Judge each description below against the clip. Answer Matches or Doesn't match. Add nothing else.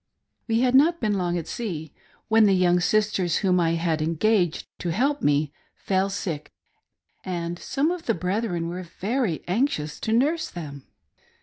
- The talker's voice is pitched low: Doesn't match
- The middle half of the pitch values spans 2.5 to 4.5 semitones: Doesn't match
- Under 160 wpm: Doesn't match